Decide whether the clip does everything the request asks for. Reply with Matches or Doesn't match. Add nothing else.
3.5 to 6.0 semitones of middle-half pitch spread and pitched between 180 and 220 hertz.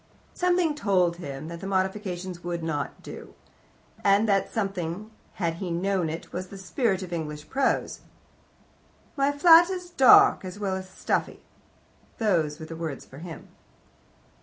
Matches